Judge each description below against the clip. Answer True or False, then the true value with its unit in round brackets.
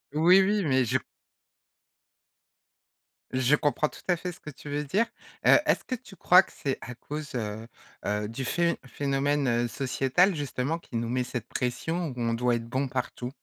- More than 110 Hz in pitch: True (135 Hz)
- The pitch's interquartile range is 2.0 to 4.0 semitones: False (4.8 semitones)